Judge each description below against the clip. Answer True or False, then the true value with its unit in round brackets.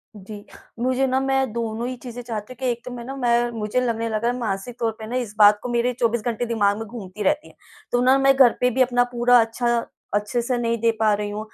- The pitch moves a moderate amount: False (2.3 semitones)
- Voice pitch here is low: False (235 Hz)